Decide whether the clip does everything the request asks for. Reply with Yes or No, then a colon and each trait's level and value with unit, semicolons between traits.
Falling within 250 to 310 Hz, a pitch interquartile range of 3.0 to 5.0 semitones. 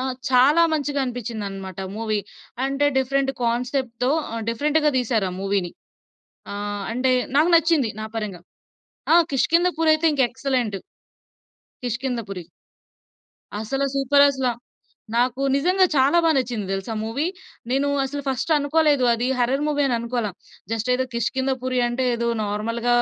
Yes: very high, 255 Hz; average, 3.6 semitones